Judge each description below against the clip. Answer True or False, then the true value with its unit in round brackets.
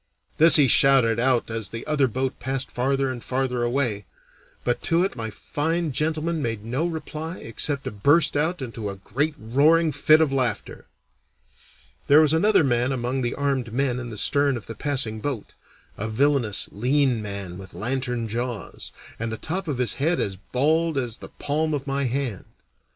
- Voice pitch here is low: True (130 Hz)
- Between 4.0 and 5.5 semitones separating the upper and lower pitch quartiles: True (4.3 semitones)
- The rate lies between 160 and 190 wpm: True (180 wpm)